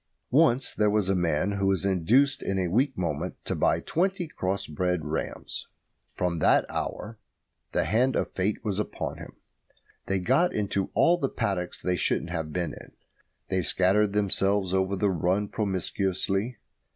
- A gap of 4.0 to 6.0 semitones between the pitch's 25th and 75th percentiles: No, average, 2.9 semitones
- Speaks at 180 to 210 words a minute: No, average, 165 wpm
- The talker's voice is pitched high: No, very low, 95 Hz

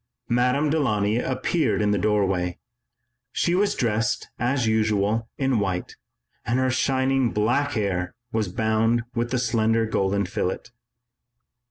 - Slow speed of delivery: Yes, slow, 130 wpm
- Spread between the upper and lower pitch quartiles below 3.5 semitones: No, average, 3.9 semitones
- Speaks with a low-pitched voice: Yes, low, 115 Hz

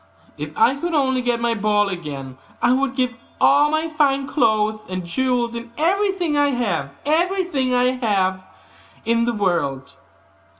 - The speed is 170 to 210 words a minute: No, average, 140 wpm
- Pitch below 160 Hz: No, high, 245 Hz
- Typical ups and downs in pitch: No, wide, 5.9 semitones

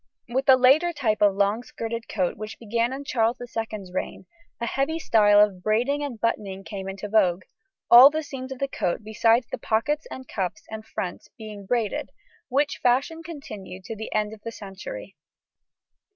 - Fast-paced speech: No, average, 180 wpm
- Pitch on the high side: Yes, high, 225 Hz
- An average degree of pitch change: Yes, average, 4.2 semitones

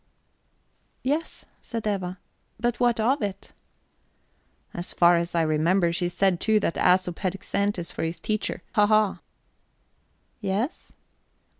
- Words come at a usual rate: No, slow, 130 wpm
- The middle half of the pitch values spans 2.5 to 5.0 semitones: Yes, average, 3.7 semitones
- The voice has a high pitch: Yes, high, 195 Hz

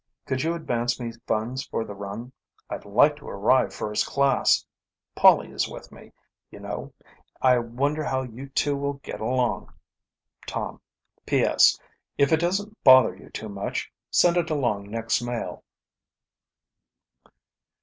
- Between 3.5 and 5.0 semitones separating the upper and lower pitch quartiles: Yes, average, 3.8 semitones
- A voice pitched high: No, low, 130 Hz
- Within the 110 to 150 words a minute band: Yes, average, 140 wpm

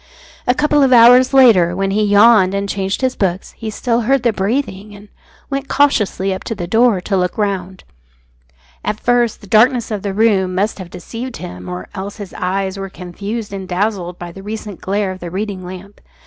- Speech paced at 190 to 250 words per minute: Yes, average, 200 wpm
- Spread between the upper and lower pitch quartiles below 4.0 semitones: Yes, average, 3.5 semitones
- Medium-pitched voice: No, high, 200 Hz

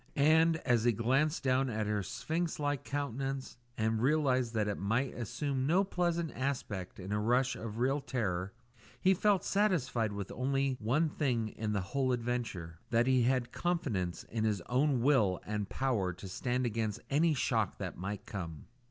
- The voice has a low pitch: Yes, low, 125 Hz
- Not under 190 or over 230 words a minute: No, average, 170 wpm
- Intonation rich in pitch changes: No, average, 4.8 semitones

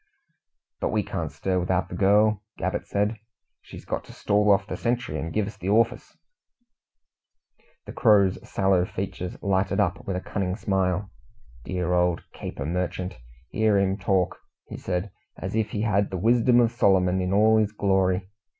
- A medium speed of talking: Yes, average, 170 wpm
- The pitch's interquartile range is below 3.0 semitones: Yes, narrow, 2.5 semitones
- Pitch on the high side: No, very low, 95 Hz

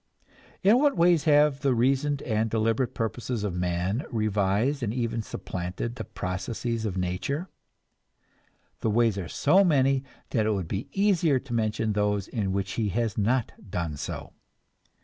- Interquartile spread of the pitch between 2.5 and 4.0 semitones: No, average, 5.2 semitones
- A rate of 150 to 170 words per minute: Yes, average, 155 wpm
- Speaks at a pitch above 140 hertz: No, low, 115 Hz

